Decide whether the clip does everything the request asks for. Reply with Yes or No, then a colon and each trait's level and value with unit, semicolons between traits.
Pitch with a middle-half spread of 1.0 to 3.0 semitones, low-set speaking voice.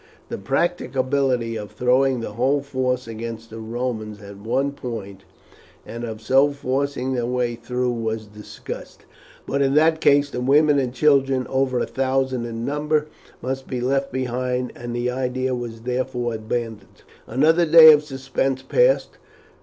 Yes: narrow, 2.6 semitones; low, 125 Hz